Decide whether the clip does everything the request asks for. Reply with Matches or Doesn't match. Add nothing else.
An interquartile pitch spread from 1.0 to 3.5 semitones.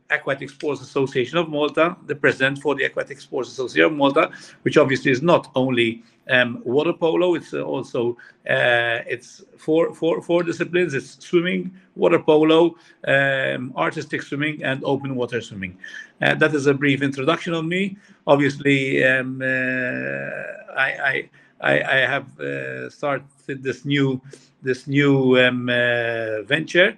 Doesn't match